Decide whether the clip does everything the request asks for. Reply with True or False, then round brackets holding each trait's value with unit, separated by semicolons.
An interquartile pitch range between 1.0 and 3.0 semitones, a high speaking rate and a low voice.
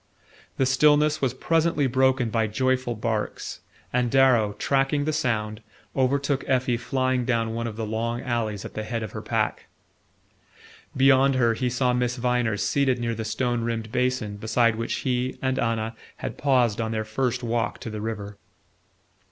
False (2.7 semitones; 170 wpm; 120 Hz)